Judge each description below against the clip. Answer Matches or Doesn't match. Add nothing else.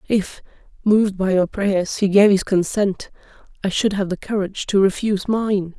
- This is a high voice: Matches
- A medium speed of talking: Matches